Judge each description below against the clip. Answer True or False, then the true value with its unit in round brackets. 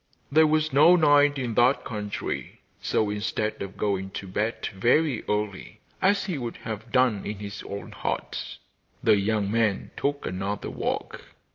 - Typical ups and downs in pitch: False (5.8 semitones)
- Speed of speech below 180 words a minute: True (155 wpm)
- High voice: False (110 Hz)